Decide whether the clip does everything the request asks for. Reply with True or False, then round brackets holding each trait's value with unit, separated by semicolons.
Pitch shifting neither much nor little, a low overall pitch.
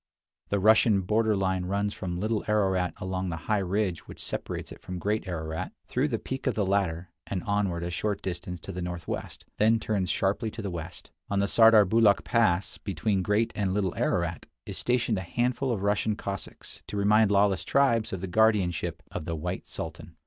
True (3.2 semitones; 100 Hz)